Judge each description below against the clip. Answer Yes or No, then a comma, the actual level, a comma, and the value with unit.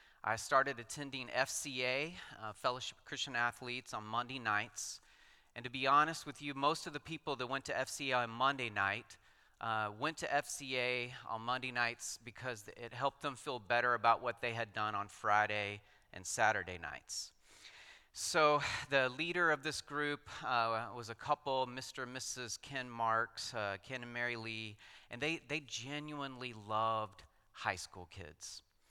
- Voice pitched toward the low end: Yes, low, 125 Hz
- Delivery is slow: No, average, 165 wpm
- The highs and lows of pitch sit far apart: No, average, 4.0 semitones